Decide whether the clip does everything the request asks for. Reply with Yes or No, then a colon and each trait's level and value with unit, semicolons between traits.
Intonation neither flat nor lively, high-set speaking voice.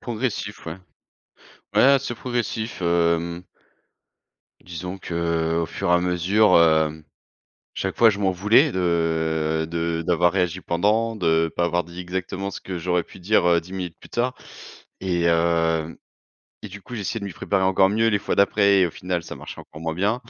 No: average, 3.3 semitones; very low, 90 Hz